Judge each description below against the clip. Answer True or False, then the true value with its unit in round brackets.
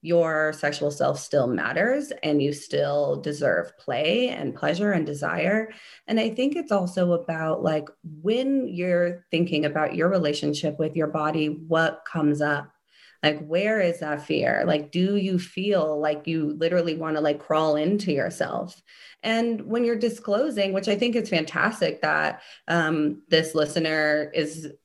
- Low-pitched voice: False (165 Hz)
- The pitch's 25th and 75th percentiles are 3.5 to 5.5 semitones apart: True (4.5 semitones)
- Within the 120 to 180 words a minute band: True (155 wpm)